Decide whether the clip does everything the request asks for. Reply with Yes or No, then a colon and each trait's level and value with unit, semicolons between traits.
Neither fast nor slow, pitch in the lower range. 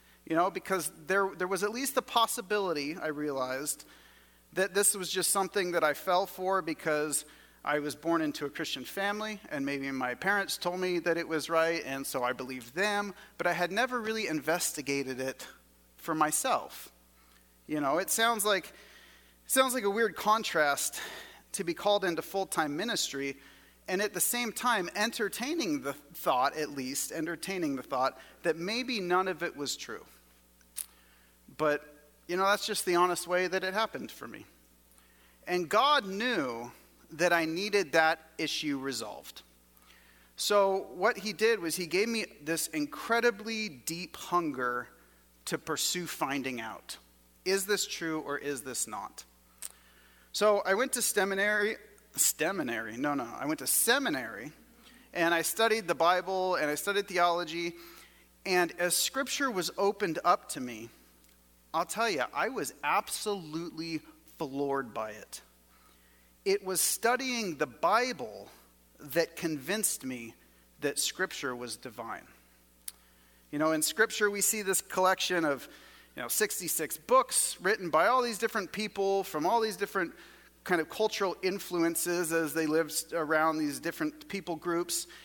No: average, 155 wpm; medium, 170 Hz